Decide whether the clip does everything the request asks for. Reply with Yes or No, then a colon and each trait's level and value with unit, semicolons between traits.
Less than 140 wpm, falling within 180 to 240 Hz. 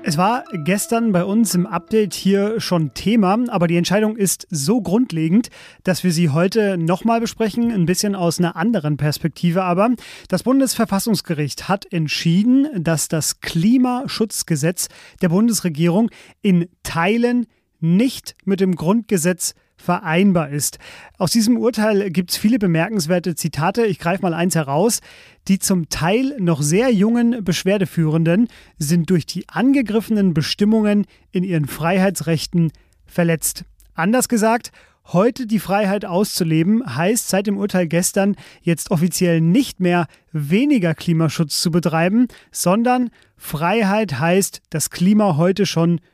Yes: average, 130 wpm; medium, 185 Hz